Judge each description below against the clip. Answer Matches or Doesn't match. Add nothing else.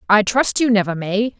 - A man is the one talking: Doesn't match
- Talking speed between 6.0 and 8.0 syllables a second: Doesn't match